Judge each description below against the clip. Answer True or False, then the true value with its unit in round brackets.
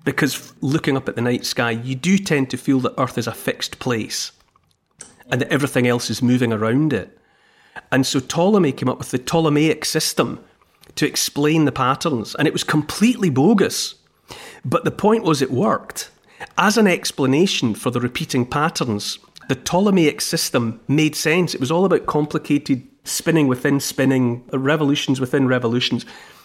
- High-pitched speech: False (140 Hz)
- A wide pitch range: False (4.0 semitones)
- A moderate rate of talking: True (165 wpm)